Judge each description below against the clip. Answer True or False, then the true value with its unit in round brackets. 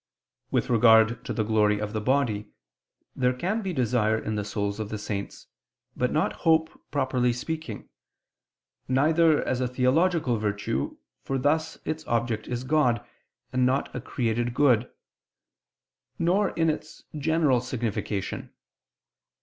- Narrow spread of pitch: False (5.6 semitones)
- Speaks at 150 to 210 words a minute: False (135 wpm)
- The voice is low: True (125 Hz)